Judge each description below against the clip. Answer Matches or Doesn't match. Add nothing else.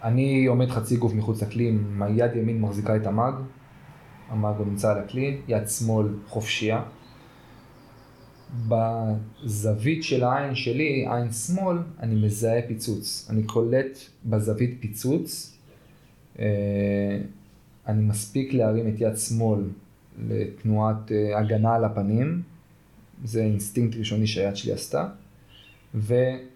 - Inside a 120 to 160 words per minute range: Doesn't match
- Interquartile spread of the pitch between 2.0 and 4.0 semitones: Matches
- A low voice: Matches